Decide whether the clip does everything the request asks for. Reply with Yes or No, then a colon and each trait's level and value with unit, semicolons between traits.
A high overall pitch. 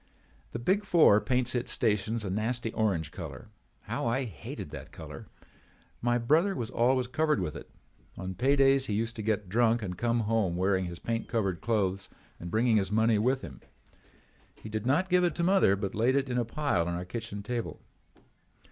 No: low, 115 Hz